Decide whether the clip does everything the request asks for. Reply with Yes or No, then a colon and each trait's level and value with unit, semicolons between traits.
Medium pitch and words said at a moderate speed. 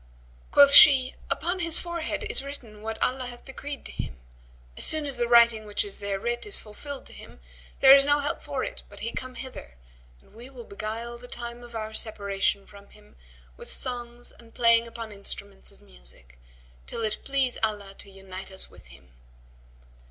No: high, 235 Hz; average, 190 wpm